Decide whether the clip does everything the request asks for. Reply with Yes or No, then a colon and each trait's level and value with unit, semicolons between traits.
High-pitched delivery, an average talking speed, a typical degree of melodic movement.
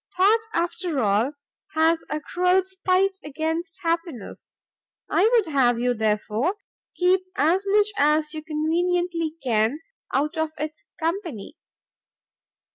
No: very high, 320 Hz; slow, 120 wpm; average, 4.1 semitones